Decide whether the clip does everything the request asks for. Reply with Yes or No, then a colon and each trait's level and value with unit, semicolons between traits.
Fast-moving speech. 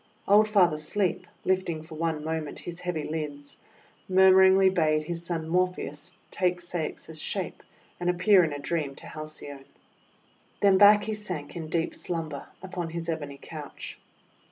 No: average, 150 wpm